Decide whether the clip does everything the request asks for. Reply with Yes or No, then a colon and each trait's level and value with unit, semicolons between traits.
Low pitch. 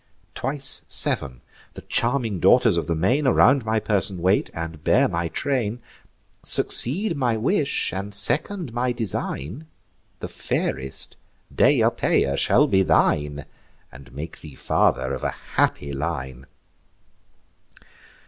Yes: low, 100 Hz